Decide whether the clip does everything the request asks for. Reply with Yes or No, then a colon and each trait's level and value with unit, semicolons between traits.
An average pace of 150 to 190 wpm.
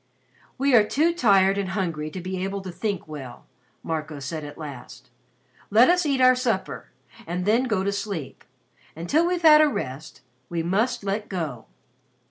Yes: average, 170 wpm